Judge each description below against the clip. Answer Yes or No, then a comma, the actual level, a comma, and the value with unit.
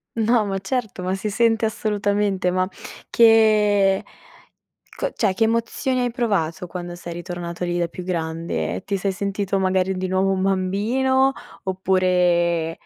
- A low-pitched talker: No, high, 195 Hz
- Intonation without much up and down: No, average, 3.2 semitones